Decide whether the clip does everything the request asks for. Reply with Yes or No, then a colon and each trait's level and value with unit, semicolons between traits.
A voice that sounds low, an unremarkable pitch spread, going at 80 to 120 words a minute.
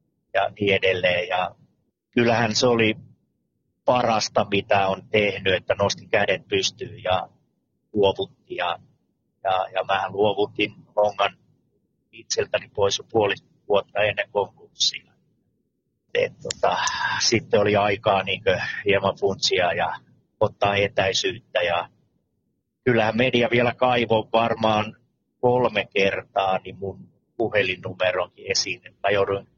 Yes: low, 105 Hz; average, 3.4 semitones; average, 110 wpm